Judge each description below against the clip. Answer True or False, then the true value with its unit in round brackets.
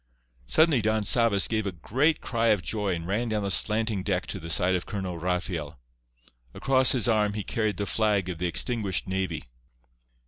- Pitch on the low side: True (100 Hz)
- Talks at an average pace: True (185 wpm)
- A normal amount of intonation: True (3.5 semitones)